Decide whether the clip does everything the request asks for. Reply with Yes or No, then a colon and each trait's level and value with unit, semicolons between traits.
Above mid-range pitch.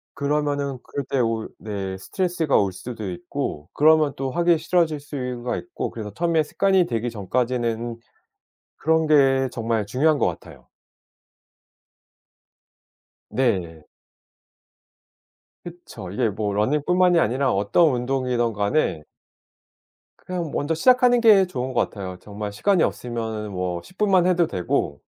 No: low, 130 Hz